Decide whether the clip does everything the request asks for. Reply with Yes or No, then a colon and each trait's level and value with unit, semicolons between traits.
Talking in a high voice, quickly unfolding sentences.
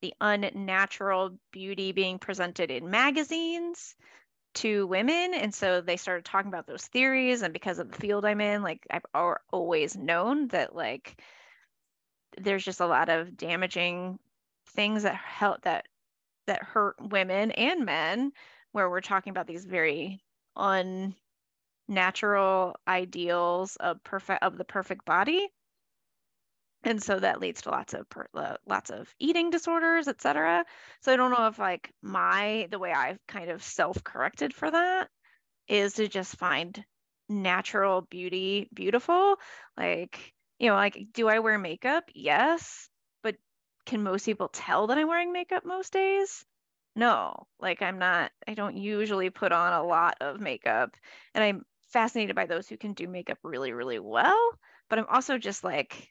No: high, 205 Hz; average, 155 wpm